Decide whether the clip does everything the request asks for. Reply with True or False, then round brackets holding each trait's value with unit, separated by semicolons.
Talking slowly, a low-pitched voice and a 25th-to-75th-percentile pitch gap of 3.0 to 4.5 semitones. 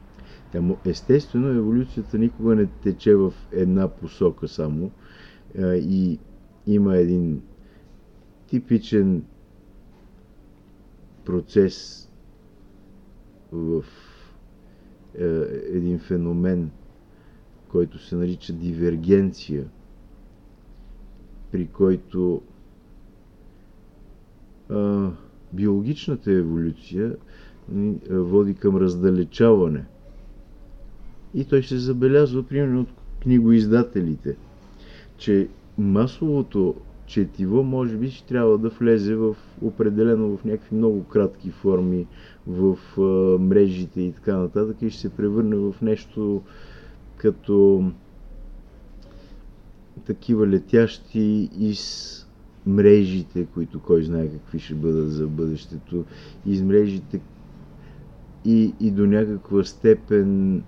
True (80 wpm; 100 Hz; 3.6 semitones)